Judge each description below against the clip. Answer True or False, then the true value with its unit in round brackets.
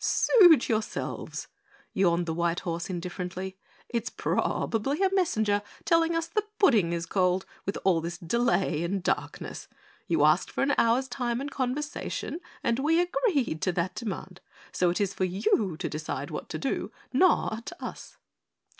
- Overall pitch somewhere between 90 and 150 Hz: False (205 Hz)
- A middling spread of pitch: False (7.6 semitones)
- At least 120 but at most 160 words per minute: True (155 wpm)